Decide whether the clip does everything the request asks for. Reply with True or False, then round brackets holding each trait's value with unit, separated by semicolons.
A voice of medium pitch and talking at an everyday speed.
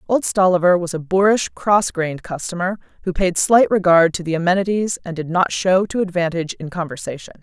True (180 Hz; 185 wpm)